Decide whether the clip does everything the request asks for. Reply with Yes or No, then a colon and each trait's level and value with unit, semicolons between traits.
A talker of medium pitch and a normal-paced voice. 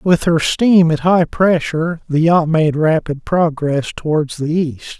Yes: medium, 160 Hz; average, 170 wpm